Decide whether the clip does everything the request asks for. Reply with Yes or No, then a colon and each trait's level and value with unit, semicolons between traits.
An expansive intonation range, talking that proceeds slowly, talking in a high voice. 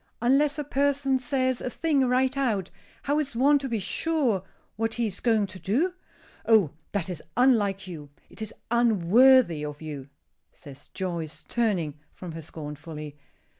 No: wide, 7.6 semitones; average, 160 wpm; high, 225 Hz